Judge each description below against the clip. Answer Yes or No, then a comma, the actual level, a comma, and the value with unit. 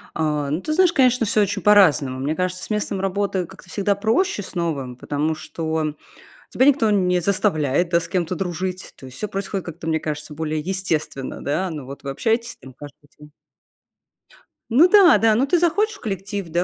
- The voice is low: No, medium, 185 Hz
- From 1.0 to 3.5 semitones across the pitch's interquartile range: No, average, 5.3 semitones